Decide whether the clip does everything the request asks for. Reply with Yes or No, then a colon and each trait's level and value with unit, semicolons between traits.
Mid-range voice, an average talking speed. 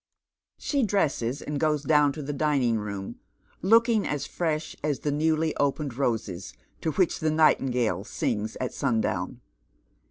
Yes: medium, 145 Hz; average, 150 wpm